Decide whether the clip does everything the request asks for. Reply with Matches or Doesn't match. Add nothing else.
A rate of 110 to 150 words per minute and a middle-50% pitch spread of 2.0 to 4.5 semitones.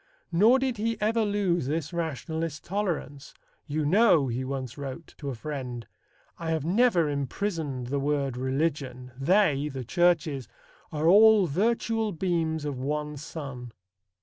Doesn't match